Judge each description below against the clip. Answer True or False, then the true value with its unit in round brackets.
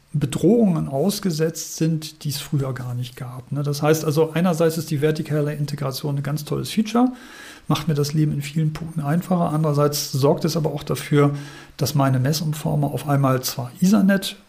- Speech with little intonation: True (2.3 semitones)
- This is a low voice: False (155 Hz)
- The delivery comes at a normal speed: True (175 wpm)